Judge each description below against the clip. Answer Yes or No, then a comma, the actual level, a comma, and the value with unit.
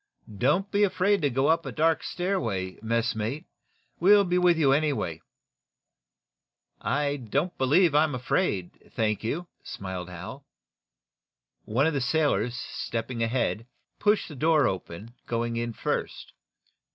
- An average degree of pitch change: No, wide, 6.3 semitones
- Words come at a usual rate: No, slow, 125 wpm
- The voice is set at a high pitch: No, low, 135 Hz